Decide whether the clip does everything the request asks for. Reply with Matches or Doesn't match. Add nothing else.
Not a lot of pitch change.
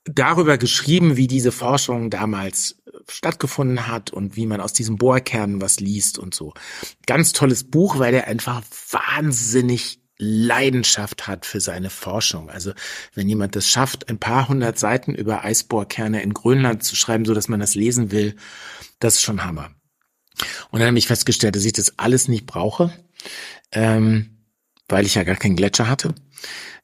Doesn't match